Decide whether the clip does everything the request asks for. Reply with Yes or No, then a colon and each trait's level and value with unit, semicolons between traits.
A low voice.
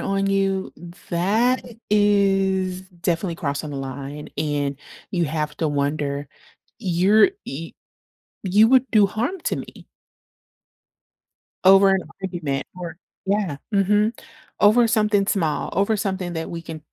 No: high, 190 Hz